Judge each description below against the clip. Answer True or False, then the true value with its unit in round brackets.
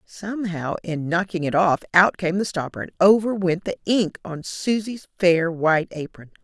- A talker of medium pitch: True (180 Hz)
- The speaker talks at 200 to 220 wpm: False (175 wpm)